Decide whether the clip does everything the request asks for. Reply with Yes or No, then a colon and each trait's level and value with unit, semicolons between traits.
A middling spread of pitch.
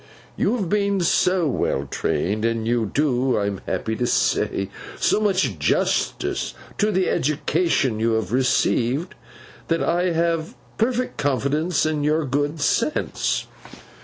No: wide, 7.0 semitones